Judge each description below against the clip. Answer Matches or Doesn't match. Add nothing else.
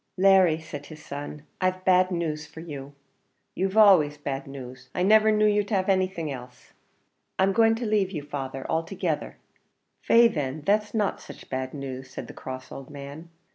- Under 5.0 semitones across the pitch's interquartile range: Doesn't match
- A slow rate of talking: Doesn't match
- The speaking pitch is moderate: Matches